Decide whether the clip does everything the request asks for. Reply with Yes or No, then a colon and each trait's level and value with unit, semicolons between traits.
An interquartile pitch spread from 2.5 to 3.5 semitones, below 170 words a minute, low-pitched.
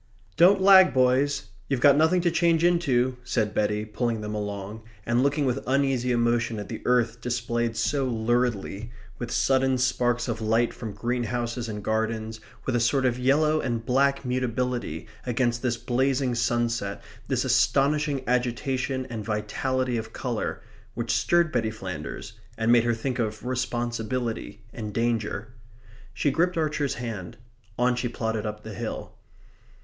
Yes: average, 2.8 semitones; average, 150 wpm; low, 120 Hz